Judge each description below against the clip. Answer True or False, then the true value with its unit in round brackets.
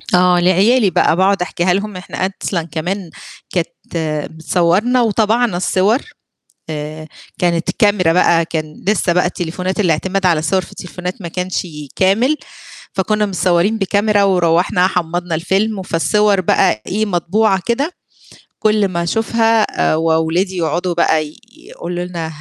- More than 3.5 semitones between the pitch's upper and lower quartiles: False (3.2 semitones)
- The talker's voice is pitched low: False (185 Hz)